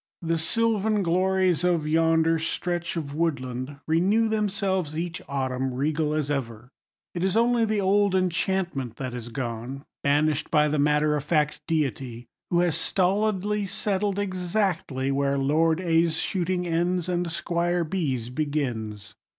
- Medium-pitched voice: Yes, medium, 165 Hz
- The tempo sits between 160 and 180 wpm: No, average, 140 wpm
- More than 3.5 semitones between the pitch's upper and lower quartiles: Yes, average, 4.8 semitones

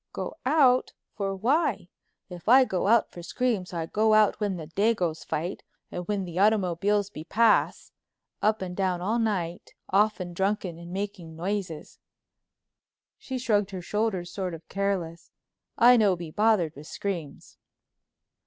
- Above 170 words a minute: No, average, 145 wpm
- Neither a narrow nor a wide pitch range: Yes, average, 3.7 semitones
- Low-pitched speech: No, high, 195 Hz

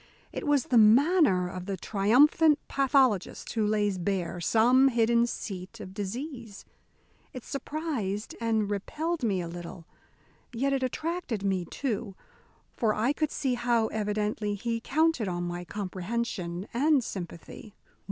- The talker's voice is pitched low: No, high, 220 Hz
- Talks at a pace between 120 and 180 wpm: Yes, slow, 135 wpm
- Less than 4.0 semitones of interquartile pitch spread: No, average, 5.3 semitones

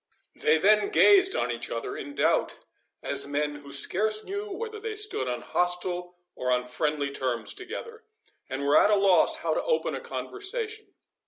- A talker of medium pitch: Yes, medium, 180 Hz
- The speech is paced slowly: No, average, 175 wpm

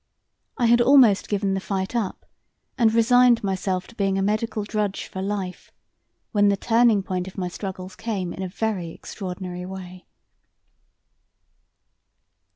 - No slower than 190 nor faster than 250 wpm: No, average, 145 wpm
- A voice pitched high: Yes, high, 195 Hz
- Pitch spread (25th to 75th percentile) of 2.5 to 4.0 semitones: Yes, average, 3.1 semitones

